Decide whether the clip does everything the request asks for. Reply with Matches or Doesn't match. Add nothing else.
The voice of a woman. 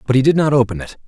Doesn't match